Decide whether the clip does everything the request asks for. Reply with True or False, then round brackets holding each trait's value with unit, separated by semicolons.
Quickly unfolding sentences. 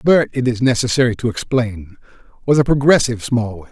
False (160 wpm)